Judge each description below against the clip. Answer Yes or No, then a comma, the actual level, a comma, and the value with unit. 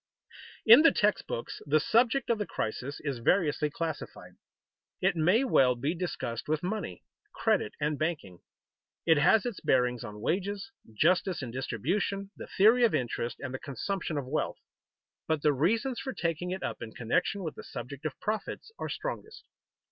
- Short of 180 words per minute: Yes, average, 170 wpm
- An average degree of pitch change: No, wide, 7.3 semitones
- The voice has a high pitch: No, medium, 160 Hz